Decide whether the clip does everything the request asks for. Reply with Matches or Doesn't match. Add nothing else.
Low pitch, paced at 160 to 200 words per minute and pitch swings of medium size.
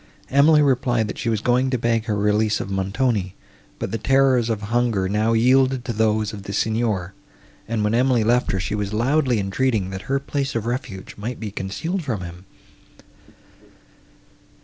Matches